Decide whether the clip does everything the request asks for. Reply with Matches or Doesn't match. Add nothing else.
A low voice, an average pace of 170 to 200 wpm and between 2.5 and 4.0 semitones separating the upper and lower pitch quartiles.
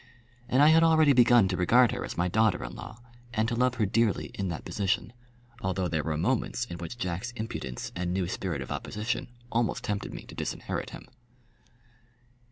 Doesn't match